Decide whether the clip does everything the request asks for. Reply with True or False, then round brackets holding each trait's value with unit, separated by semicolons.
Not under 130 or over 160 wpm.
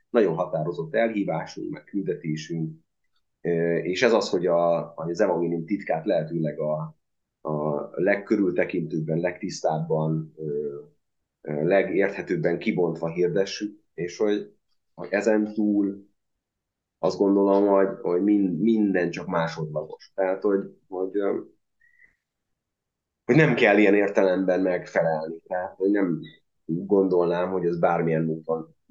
False (105 wpm)